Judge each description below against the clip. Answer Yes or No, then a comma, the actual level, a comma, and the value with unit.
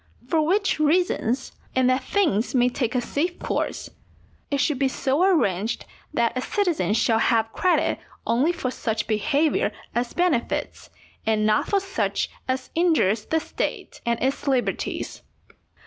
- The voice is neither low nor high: No, very high, 260 Hz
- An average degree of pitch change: No, wide, 5.7 semitones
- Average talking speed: Yes, average, 150 wpm